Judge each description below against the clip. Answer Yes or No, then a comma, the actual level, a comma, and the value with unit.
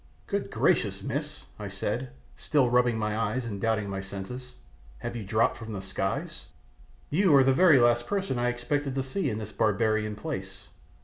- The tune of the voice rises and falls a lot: No, average, 3.8 semitones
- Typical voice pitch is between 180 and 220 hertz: No, low, 115 Hz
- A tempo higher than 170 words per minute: Yes, average, 180 wpm